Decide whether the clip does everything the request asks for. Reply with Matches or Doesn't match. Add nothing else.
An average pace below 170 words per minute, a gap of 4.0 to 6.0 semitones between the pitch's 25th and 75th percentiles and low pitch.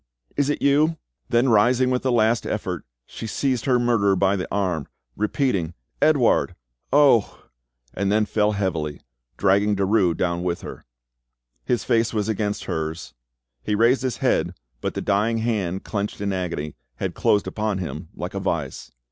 Matches